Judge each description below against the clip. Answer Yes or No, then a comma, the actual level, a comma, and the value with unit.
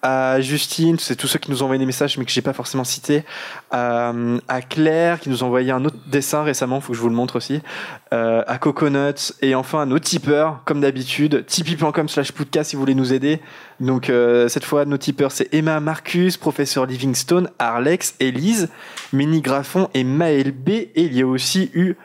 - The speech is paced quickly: No, average, 200 wpm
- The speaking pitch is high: No, medium, 140 Hz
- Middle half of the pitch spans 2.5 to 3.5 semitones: Yes, average, 3.2 semitones